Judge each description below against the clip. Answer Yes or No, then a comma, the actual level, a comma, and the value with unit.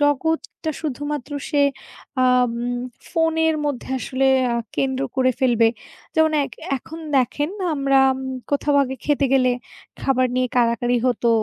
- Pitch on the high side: Yes, very high, 270 Hz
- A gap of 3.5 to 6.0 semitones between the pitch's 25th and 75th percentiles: No, average, 2.7 semitones